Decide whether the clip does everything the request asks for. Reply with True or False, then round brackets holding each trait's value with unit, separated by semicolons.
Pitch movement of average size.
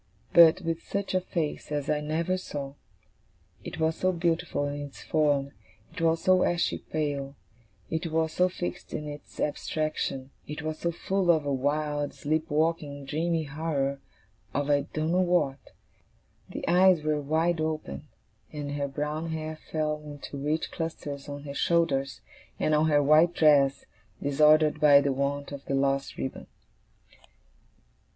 False (2.3 semitones)